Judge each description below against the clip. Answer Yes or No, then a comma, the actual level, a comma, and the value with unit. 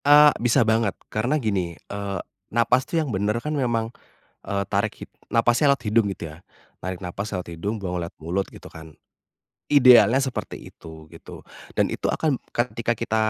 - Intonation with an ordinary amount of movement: Yes, average, 4.1 semitones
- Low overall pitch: Yes, low, 110 Hz